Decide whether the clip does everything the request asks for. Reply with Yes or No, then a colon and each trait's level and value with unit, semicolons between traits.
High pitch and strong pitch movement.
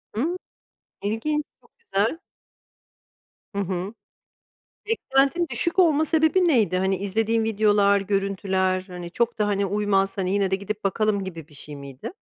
No: high, 205 Hz; average, 4.0 semitones